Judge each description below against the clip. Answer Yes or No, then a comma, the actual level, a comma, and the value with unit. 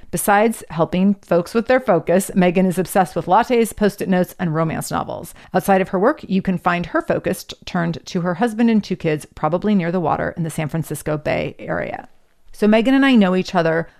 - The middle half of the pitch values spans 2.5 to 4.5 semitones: Yes, average, 3.3 semitones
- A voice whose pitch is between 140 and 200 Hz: Yes, medium, 185 Hz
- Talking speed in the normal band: No, fast, 215 wpm